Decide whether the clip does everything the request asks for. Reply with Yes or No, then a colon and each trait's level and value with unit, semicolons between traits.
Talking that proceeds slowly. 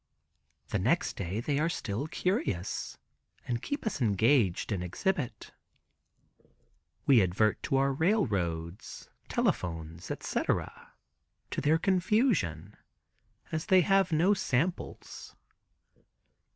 Yes: slow, 100 wpm